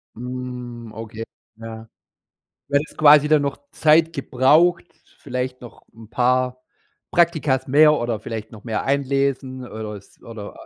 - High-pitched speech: No, low, 125 Hz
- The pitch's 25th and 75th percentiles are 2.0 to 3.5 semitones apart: No, average, 3.9 semitones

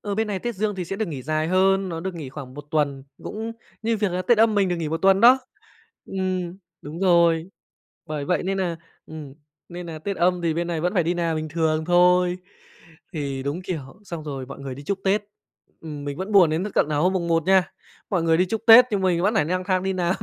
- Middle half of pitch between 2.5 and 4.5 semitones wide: Yes, average, 3.4 semitones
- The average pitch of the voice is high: No, medium, 175 Hz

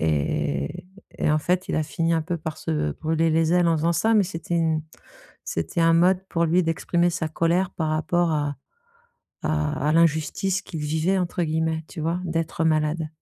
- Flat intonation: Yes, narrow, 1.8 semitones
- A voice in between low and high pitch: Yes, medium, 165 Hz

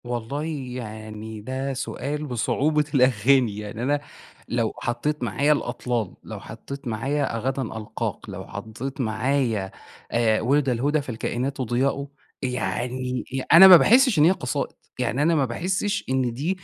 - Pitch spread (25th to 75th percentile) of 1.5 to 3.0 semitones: No, average, 3.7 semitones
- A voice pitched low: Yes, low, 130 Hz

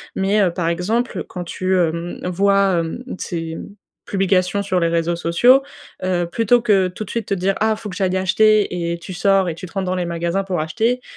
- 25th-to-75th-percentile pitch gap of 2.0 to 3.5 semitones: Yes, average, 2.7 semitones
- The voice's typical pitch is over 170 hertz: Yes, medium, 185 Hz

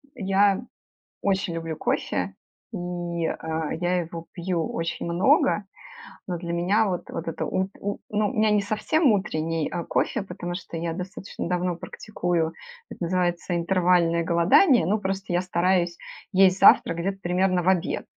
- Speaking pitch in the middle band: Yes, medium, 180 Hz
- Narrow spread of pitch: Yes, narrow, 2.2 semitones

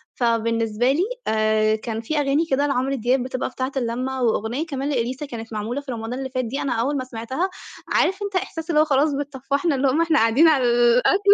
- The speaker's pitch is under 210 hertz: No, very high, 260 Hz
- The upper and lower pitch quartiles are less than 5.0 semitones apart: Yes, average, 3.7 semitones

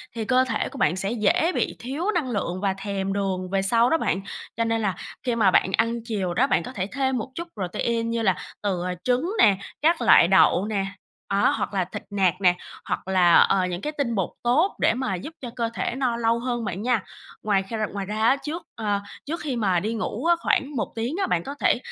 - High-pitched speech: Yes, high, 220 Hz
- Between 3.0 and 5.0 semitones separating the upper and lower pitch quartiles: Yes, average, 4.6 semitones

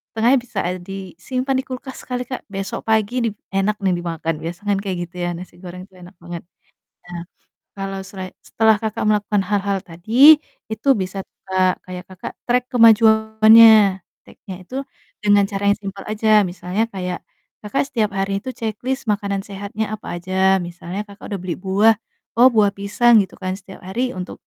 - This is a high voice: Yes, high, 200 Hz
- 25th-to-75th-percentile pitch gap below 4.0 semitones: Yes, average, 2.8 semitones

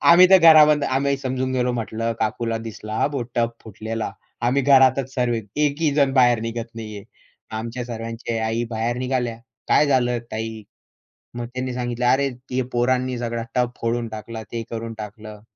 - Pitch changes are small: Yes, narrow, 2.3 semitones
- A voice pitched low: Yes, low, 120 Hz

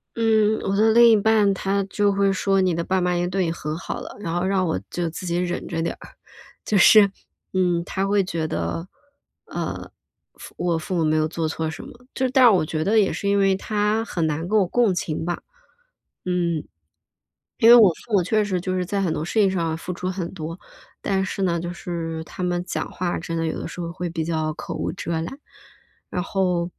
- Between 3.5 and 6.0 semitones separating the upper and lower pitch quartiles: No, average, 3.0 semitones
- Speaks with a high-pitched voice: No, medium, 180 Hz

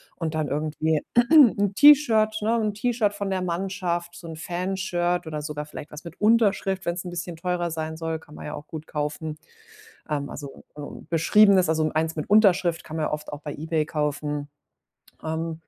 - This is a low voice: No, medium, 165 Hz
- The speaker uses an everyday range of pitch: Yes, average, 3.9 semitones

